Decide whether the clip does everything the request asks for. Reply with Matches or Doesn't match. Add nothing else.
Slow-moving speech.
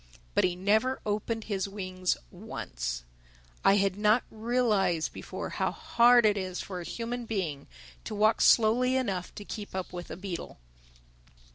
Doesn't match